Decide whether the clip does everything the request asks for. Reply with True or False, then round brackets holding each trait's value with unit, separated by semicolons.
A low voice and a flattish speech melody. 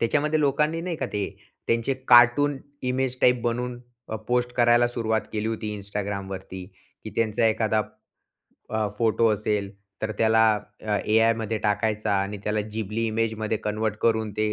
True (110 Hz; 2.2 semitones)